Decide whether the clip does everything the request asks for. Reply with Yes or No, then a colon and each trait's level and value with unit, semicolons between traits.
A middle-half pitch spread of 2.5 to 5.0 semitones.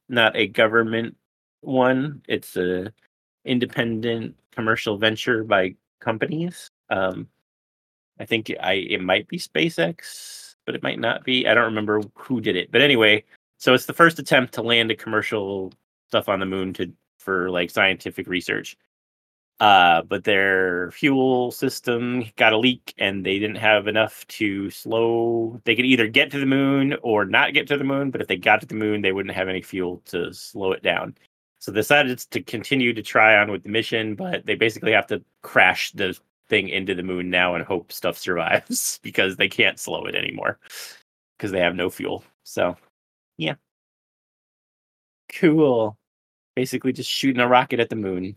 Yes: average, 4.7 semitones